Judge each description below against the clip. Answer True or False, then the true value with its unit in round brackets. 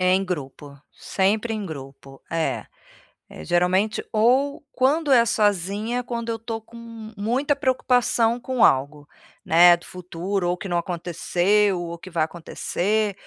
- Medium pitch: False (195 Hz)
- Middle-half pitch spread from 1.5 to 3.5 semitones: False (4.9 semitones)